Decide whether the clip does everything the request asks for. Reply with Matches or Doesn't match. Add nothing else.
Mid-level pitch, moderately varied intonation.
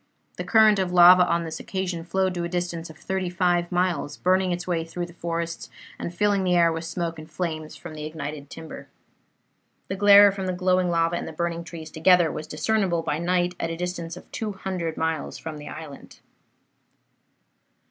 Doesn't match